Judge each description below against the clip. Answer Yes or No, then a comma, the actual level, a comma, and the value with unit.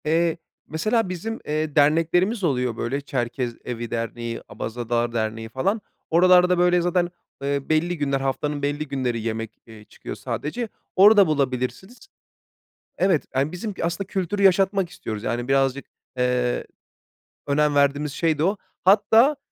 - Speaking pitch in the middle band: Yes, medium, 150 Hz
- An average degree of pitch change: No, wide, 6.2 semitones